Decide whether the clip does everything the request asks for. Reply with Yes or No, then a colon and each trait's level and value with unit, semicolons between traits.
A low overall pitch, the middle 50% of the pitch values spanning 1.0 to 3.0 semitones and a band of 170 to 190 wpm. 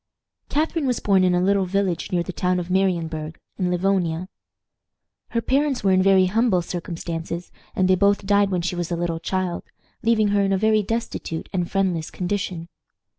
No: medium, 185 Hz; narrow, 2.4 semitones; average, 180 wpm